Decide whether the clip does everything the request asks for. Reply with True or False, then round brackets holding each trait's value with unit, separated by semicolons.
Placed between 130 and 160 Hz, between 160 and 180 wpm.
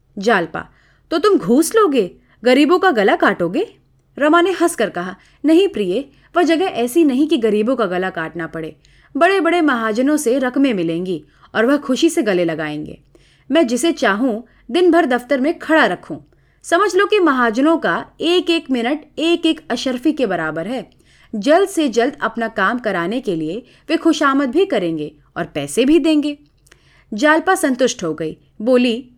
False (260 Hz; 165 wpm)